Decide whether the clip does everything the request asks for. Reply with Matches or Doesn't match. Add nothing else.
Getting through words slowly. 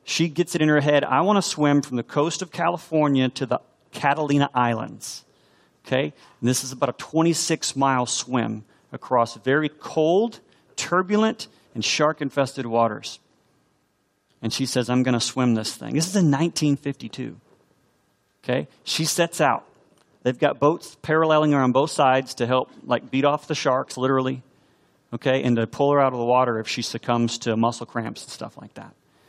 Doesn't match